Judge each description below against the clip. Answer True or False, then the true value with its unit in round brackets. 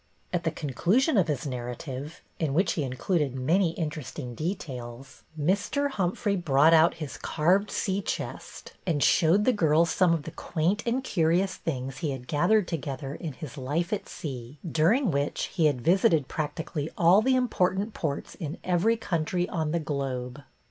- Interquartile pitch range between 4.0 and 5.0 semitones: True (4.5 semitones)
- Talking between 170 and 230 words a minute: True (175 wpm)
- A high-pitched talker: False (160 Hz)